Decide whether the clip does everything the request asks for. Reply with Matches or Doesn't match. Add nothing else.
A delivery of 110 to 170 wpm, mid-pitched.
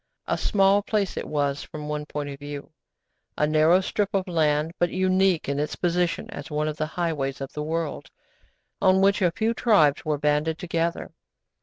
Doesn't match